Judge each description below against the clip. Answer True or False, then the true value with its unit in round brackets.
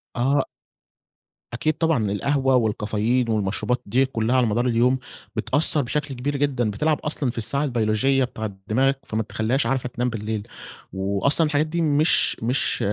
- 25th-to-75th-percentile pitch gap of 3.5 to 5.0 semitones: True (4.2 semitones)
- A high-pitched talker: False (125 Hz)